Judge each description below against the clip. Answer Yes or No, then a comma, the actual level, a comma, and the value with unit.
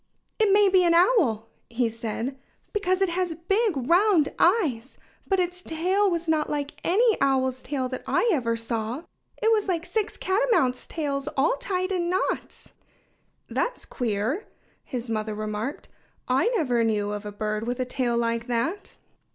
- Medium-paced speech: Yes, average, 160 wpm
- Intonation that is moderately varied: No, wide, 7.9 semitones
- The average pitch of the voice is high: Yes, very high, 290 Hz